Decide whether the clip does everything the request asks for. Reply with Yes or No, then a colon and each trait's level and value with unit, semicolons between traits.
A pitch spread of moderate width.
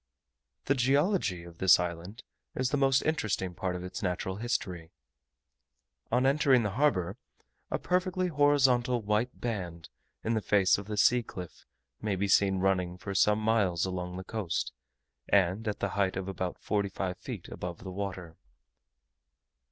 Yes: average, 5.0 semitones